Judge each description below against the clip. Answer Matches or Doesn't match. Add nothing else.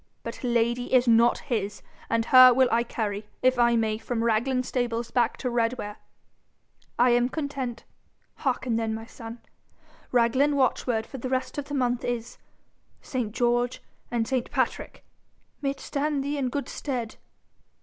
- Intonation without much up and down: Matches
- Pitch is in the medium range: Doesn't match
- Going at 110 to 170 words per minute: Matches